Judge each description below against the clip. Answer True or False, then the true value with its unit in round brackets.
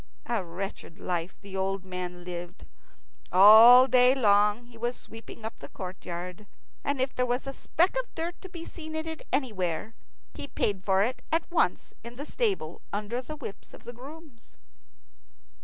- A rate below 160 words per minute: False (175 wpm)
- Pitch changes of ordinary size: False (6.2 semitones)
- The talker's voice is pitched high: True (230 Hz)